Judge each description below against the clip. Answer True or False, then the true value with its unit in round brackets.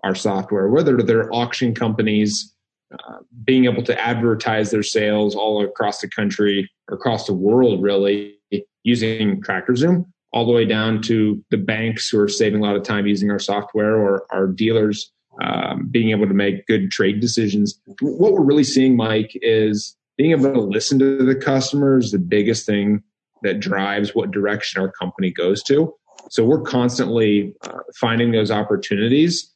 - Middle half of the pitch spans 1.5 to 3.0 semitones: True (2.7 semitones)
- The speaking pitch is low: True (110 Hz)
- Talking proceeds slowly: False (170 wpm)